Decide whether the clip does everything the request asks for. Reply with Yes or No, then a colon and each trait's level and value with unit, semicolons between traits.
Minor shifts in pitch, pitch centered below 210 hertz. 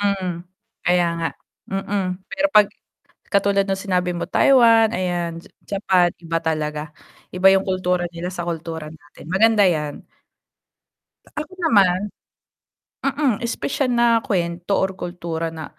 No: average, 3.4 semitones; medium, 185 Hz